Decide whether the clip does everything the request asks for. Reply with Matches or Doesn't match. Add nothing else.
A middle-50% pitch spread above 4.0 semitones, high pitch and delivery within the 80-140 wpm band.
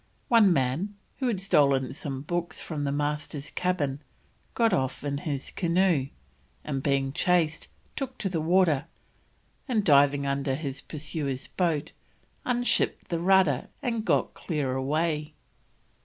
Doesn't match